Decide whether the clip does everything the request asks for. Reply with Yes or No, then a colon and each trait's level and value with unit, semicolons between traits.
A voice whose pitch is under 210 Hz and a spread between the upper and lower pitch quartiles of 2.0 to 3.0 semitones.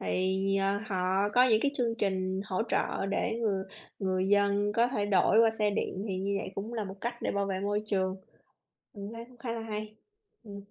Yes: high, 200 Hz; narrow, 2.5 semitones